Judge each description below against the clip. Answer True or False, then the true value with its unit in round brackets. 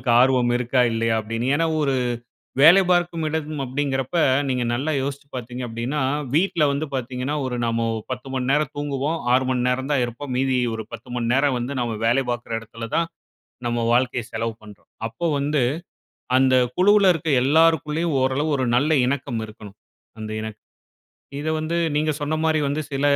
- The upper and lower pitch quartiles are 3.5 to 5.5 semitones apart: True (3.8 semitones)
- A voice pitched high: False (135 Hz)